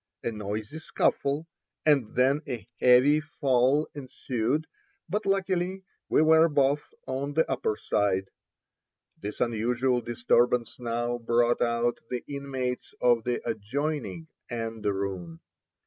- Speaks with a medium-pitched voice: No, low, 125 Hz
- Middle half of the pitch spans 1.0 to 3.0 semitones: No, average, 3.8 semitones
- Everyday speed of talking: No, slow, 115 wpm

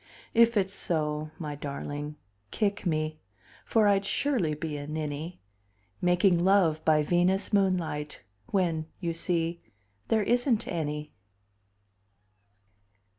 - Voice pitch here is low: No, medium, 170 Hz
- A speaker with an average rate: No, slow, 110 wpm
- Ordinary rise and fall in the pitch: Yes, average, 4.4 semitones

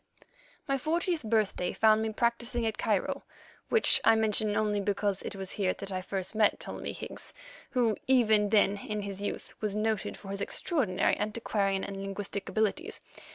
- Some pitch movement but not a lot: No, narrow, 2.2 semitones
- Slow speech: No, average, 165 wpm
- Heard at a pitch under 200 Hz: No, high, 210 Hz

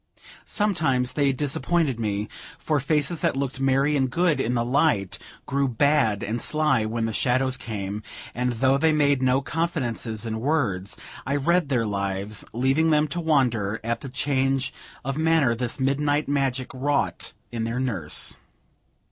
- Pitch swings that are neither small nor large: Yes, average, 4.0 semitones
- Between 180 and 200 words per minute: No, average, 155 wpm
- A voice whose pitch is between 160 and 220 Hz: No, low, 130 Hz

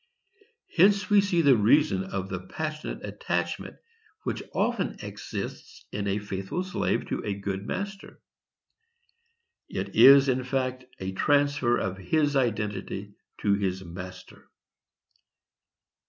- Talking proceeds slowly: Yes, slow, 120 wpm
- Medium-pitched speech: No, low, 120 Hz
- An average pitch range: No, wide, 7.7 semitones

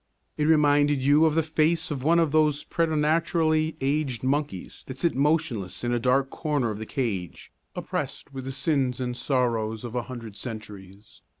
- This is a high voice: No, low, 135 Hz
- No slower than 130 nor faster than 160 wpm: No, average, 175 wpm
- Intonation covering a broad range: No, average, 4.3 semitones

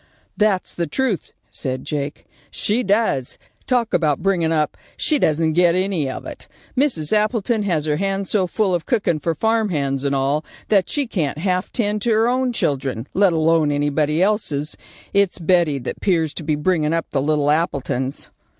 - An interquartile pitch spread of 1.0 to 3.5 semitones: No, wide, 5.5 semitones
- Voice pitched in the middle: Yes, medium, 170 Hz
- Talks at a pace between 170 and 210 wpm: Yes, average, 175 wpm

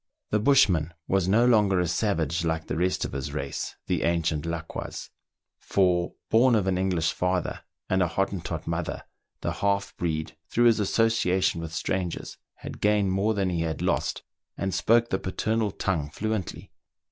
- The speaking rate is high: No, average, 170 wpm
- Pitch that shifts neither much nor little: Yes, average, 3.9 semitones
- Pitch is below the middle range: Yes, very low, 95 Hz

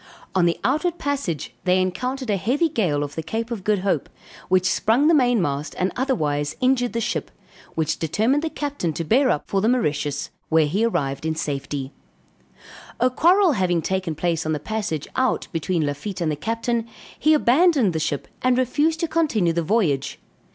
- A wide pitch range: Yes, wide, 8.1 semitones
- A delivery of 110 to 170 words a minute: No, average, 185 wpm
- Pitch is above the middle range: Yes, high, 195 Hz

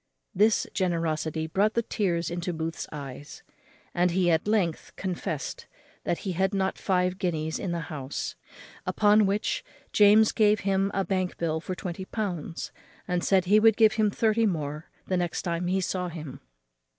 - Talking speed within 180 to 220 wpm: No, average, 165 wpm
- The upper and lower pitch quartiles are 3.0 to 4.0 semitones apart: Yes, average, 3.5 semitones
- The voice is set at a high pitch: No, medium, 180 Hz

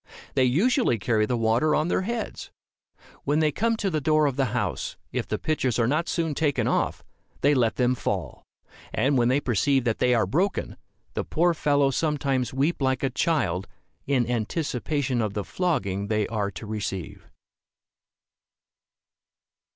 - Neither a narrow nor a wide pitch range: Yes, average, 4.8 semitones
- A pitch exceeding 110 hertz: Yes, low, 135 Hz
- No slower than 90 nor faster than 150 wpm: No, average, 165 wpm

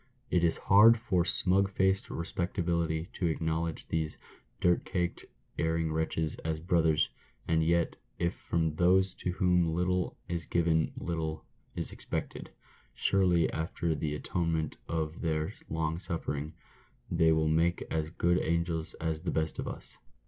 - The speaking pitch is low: Yes, very low, 85 Hz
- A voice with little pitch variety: Yes, narrow, 1.7 semitones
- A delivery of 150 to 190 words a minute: No, average, 140 wpm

